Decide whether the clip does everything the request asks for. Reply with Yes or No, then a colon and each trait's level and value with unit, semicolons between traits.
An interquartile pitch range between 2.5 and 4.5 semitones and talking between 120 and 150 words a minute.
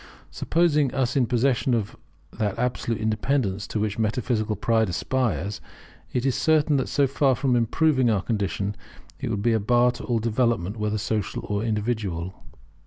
No: average, 3.4 semitones; average, 165 wpm